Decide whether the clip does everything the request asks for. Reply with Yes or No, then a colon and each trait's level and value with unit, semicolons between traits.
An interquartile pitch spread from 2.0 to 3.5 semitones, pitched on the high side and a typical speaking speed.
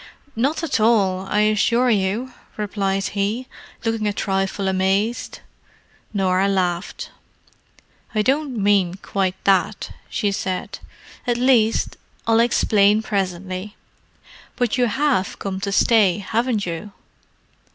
No: average, 3.0 semitones; high, 205 Hz; slow, 110 wpm